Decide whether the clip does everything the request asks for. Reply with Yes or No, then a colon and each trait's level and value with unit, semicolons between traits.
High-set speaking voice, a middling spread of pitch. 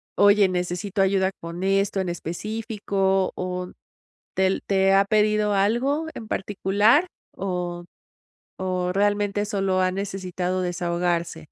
No: high, 195 Hz; narrow, 2.1 semitones